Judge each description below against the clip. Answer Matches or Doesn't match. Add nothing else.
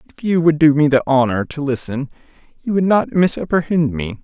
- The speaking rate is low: Doesn't match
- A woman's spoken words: Doesn't match